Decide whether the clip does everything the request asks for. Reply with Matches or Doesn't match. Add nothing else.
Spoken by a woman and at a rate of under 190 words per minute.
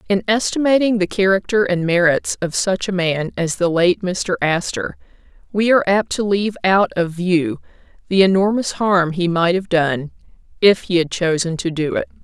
Matches